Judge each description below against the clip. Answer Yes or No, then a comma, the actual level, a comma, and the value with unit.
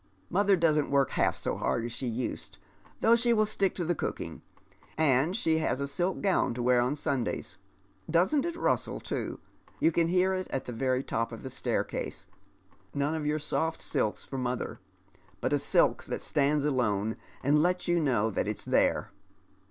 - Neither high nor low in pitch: Yes, medium, 150 Hz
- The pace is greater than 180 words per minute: Yes, average, 195 wpm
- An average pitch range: No, wide, 5.7 semitones